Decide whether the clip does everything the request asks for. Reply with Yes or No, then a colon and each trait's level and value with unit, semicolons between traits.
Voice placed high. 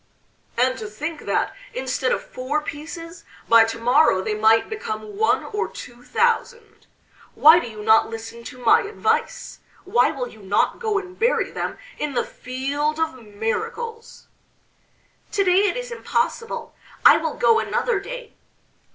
Yes: very high, 305 Hz